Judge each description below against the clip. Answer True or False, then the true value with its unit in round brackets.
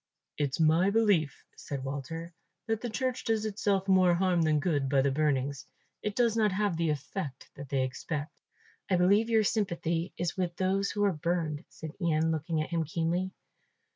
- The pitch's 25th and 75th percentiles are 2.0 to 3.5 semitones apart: False (4.5 semitones)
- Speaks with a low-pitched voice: False (170 Hz)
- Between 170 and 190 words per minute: True (180 wpm)